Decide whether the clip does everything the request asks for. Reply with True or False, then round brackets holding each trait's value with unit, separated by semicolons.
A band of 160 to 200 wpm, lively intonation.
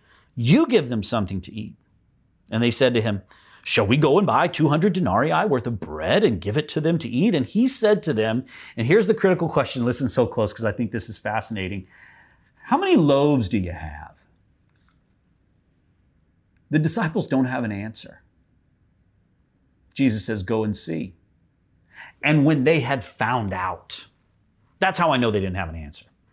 True (180 wpm; 6.7 semitones)